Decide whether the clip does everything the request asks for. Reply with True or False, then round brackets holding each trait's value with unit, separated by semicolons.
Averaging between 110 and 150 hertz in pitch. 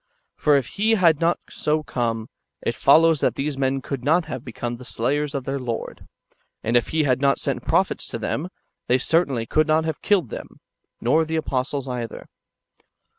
True (140 Hz)